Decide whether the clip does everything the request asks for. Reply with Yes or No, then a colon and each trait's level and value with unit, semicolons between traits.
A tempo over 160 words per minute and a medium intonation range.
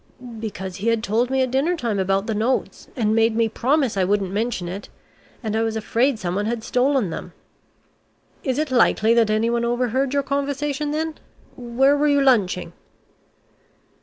Yes: average, 170 wpm; average, 3.9 semitones